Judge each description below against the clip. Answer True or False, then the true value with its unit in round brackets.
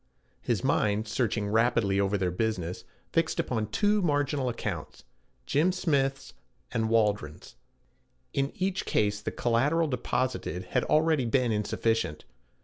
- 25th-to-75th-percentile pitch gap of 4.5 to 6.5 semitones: True (5.1 semitones)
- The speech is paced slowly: True (125 wpm)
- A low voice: True (115 Hz)